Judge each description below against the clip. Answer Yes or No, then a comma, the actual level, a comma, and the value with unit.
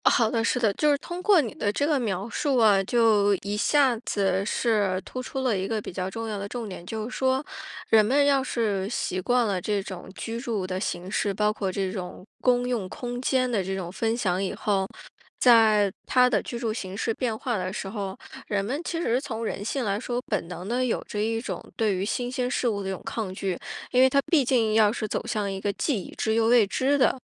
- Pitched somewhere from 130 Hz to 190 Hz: No, high, 220 Hz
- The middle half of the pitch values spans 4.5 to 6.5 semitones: No, average, 3.9 semitones